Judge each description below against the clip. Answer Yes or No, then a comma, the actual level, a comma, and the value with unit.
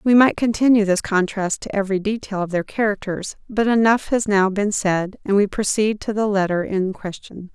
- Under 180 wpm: No, average, 200 wpm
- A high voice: Yes, high, 205 Hz